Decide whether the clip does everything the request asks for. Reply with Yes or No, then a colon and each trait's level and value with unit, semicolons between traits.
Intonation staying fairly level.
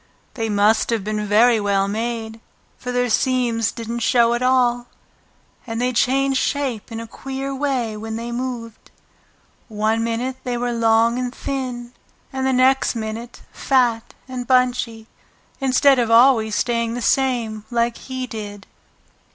Yes: narrow, 2.2 semitones